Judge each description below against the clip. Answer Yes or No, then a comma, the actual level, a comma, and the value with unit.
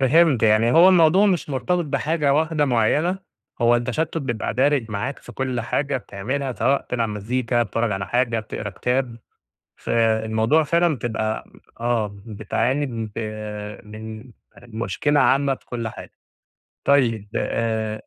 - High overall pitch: No, low, 120 Hz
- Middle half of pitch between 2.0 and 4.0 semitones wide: No, average, 4.4 semitones